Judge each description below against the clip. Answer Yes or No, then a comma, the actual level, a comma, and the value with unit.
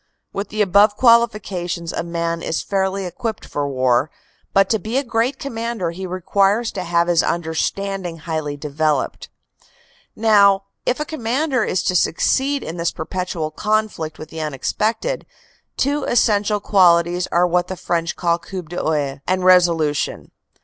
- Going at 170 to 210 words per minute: No, average, 150 wpm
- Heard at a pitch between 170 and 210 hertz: Yes, medium, 185 Hz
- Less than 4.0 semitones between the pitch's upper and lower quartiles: No, average, 4.3 semitones